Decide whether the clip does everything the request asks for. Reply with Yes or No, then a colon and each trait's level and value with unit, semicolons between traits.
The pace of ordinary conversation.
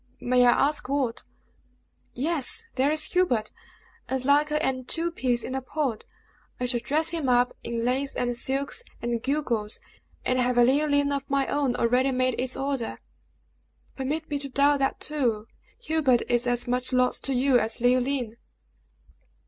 Yes: average, 165 wpm